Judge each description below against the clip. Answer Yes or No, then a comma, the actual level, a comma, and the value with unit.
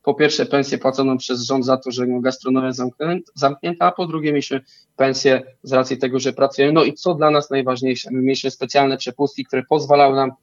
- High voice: No, low, 135 Hz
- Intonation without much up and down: Yes, narrow, 1.8 semitones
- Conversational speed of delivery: No, fast, 195 wpm